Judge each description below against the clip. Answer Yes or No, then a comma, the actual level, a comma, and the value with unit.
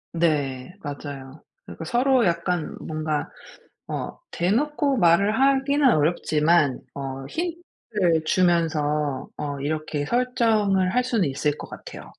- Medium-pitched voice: Yes, medium, 170 Hz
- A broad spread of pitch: Yes, wide, 7.7 semitones